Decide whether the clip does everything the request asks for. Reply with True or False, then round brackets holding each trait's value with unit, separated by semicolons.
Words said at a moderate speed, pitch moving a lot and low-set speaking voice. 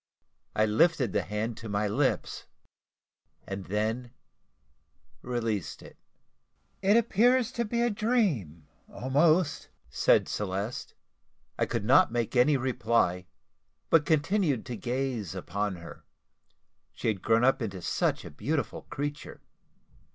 False (120 wpm; 6.7 semitones; 120 Hz)